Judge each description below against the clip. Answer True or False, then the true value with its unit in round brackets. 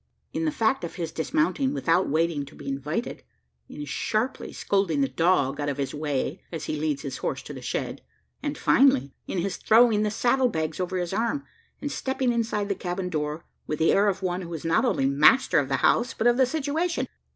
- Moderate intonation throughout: False (7.9 semitones)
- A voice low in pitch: False (185 Hz)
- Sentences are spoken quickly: True (215 wpm)